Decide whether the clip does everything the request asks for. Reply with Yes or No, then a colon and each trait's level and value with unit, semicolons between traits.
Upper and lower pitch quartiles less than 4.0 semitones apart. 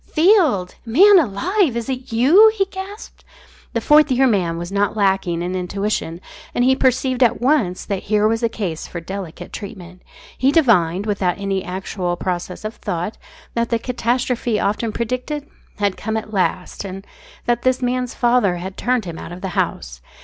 No: average, 5.3 semitones